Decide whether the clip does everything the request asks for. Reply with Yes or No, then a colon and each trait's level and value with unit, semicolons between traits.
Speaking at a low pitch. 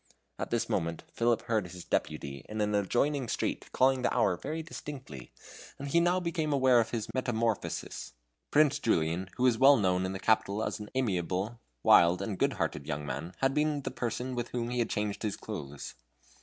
Yes: low, 115 Hz